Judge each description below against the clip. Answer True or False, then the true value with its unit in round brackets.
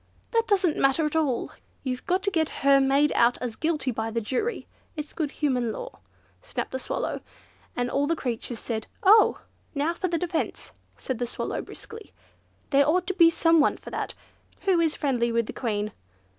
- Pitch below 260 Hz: False (290 Hz)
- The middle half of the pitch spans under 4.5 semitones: False (5.4 semitones)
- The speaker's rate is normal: True (185 wpm)